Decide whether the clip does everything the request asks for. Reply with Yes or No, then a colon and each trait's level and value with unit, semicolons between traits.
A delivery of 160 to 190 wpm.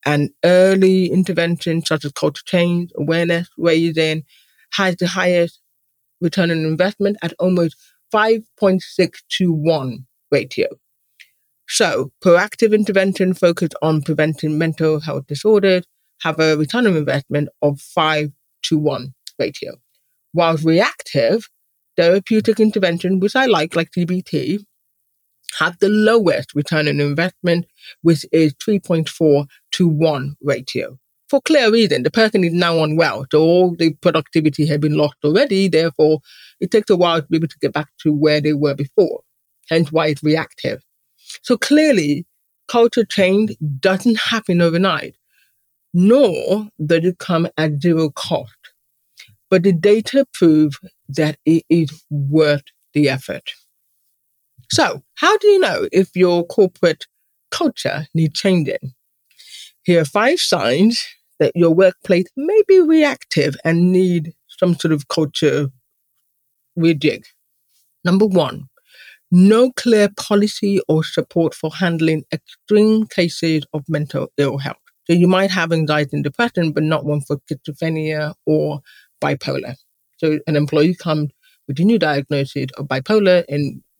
No: slow, 135 wpm